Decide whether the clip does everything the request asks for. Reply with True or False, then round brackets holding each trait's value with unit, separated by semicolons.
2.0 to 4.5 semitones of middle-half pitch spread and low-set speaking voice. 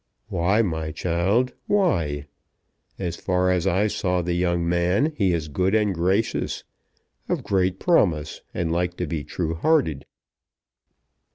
True (2.7 semitones; 90 Hz)